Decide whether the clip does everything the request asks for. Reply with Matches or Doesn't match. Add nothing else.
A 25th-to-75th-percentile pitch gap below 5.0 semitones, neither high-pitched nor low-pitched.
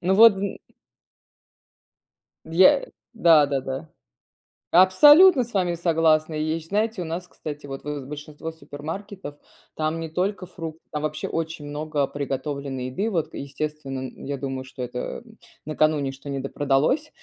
Matches